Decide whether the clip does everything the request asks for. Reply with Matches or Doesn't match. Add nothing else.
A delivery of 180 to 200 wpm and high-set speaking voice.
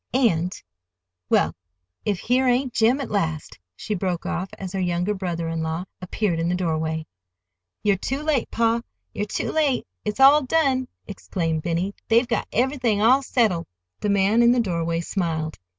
Doesn't match